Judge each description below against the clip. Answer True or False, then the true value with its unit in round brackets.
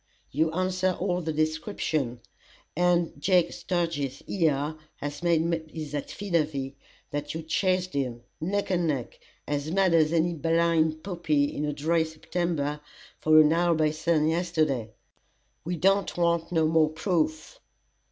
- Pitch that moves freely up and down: False (2.4 semitones)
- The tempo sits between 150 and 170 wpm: False (140 wpm)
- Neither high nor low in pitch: True (160 Hz)